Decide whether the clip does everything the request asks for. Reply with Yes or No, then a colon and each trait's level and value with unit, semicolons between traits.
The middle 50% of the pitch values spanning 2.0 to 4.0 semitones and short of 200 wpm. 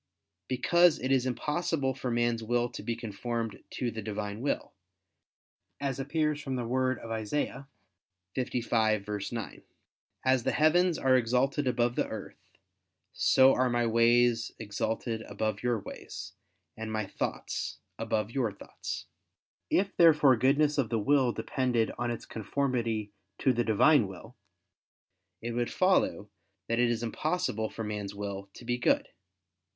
Yes: average, 3.1 semitones; average, 145 wpm